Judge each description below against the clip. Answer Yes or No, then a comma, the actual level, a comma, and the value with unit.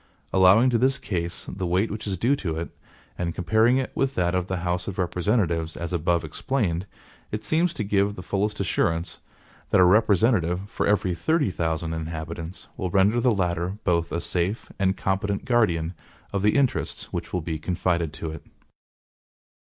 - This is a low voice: Yes, very low, 90 Hz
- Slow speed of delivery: No, average, 175 wpm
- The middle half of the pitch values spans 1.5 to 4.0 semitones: Yes, average, 3.7 semitones